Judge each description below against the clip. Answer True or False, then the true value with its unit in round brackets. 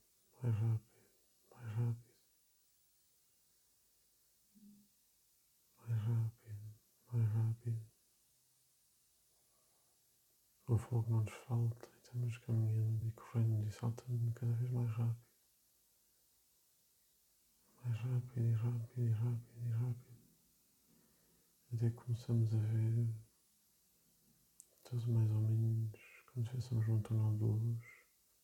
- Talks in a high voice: False (115 Hz)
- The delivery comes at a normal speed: False (95 wpm)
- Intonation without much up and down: True (1.2 semitones)